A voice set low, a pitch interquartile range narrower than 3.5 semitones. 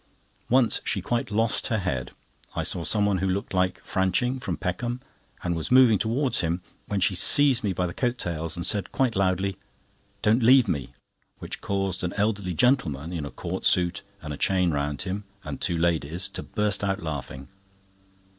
No: very low, 95 Hz; average, 4.5 semitones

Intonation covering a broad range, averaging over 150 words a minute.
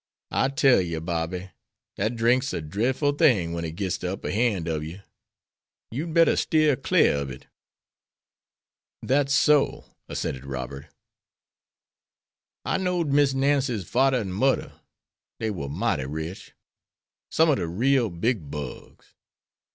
No: wide, 8.6 semitones; slow, 135 wpm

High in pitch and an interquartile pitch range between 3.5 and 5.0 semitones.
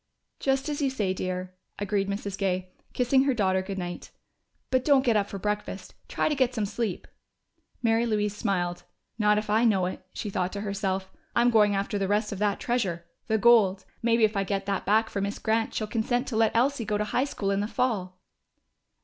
No: high, 210 Hz; average, 3.0 semitones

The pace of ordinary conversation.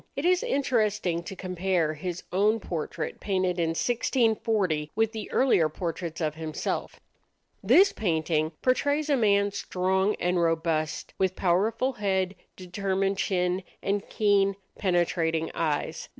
No: slow, 125 wpm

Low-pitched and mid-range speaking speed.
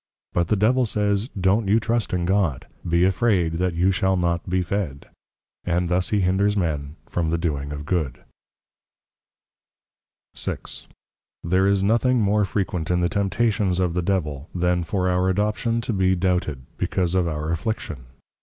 Yes: very low, 90 Hz; average, 165 wpm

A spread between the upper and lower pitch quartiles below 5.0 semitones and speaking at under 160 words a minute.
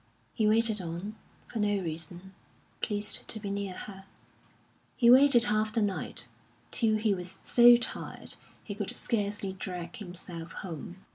Yes: average, 3.1 semitones; average, 145 wpm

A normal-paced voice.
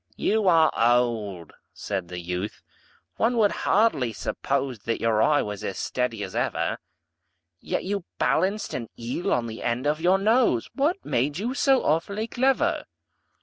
Yes: average, 155 wpm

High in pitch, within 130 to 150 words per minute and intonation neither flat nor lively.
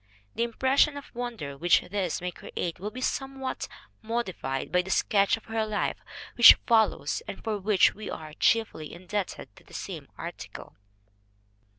No: high, 215 Hz; average, 160 wpm; average, 4.7 semitones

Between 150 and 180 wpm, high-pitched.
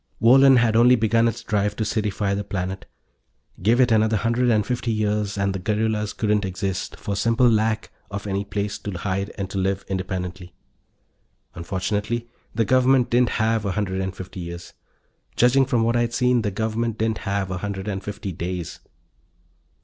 No: average, 175 wpm; low, 105 Hz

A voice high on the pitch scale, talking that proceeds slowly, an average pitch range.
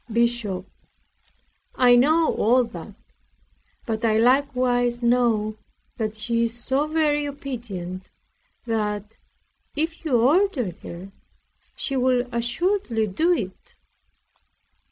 Yes: high, 240 Hz; slow, 100 wpm; average, 4.1 semitones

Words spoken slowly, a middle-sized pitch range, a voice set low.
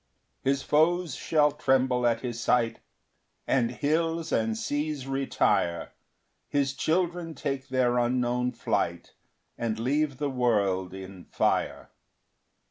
Yes: slow, 120 wpm; average, 3.9 semitones; low, 130 Hz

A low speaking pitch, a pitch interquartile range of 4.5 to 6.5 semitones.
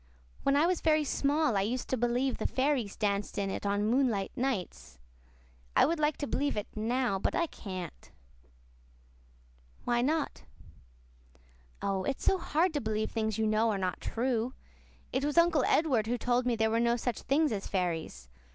No: high, 240 Hz; average, 5.1 semitones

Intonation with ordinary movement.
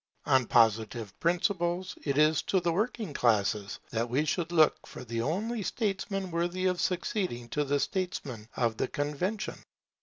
No: wide, 7.5 semitones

